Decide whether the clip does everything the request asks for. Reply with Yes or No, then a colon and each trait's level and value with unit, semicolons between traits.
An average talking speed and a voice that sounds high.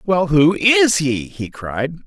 No: average, 175 wpm; medium, 160 Hz